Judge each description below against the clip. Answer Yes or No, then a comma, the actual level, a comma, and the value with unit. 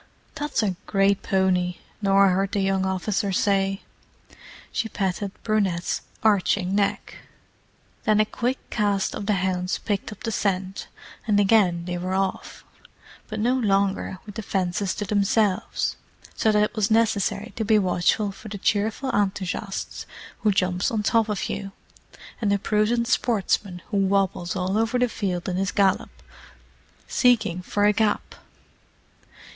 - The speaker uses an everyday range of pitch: No, narrow, 2.1 semitones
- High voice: Yes, high, 200 Hz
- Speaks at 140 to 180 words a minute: Yes, average, 150 wpm